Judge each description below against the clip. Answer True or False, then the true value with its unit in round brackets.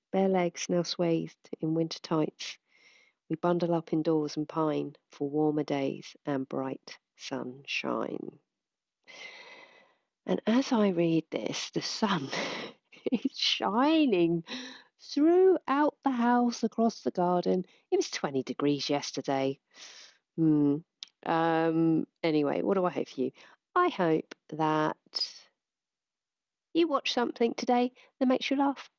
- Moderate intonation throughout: False (8.4 semitones)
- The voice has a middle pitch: True (175 Hz)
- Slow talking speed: True (120 wpm)